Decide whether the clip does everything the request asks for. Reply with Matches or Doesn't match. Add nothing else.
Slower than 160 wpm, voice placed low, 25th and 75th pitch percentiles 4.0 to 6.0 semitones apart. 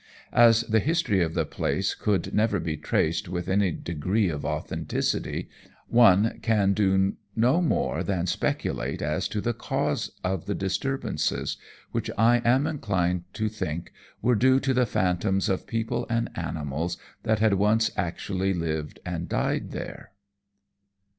Matches